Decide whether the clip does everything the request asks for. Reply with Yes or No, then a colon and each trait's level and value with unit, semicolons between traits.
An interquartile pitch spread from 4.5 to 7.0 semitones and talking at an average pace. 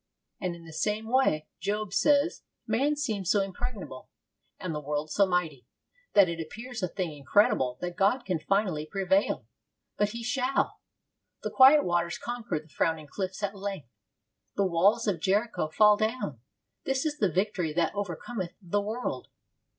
Yes: average, 4.8 semitones; average, 160 wpm